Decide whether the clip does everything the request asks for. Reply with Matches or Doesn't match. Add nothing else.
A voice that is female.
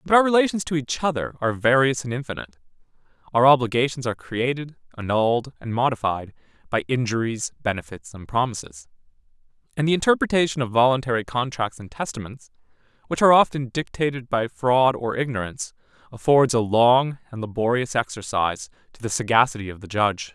Doesn't match